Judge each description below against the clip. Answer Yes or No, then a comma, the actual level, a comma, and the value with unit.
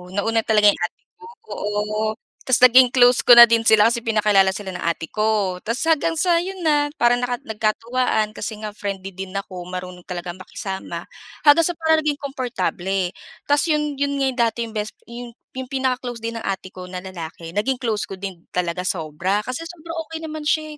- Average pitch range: No, wide, 5.7 semitones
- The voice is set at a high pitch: Yes, high, 225 Hz